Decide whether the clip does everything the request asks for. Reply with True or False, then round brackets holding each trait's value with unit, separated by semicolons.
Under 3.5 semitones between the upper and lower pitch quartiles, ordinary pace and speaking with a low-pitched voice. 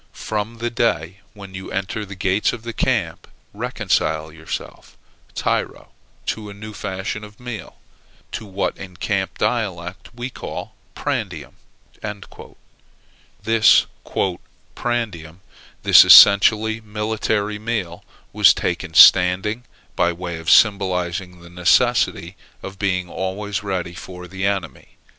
False (3.1 semitones; 120 wpm; 100 Hz)